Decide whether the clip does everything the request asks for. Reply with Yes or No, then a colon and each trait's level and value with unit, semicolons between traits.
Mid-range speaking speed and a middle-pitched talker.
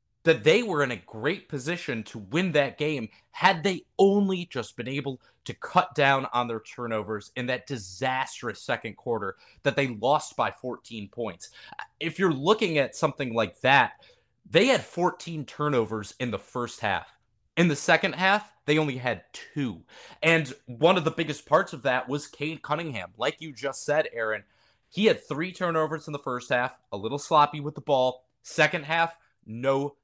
Yes: average, 180 wpm; medium, 145 Hz